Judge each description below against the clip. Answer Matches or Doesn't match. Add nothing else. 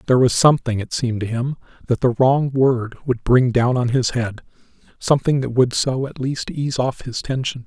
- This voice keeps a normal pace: Doesn't match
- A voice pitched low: Matches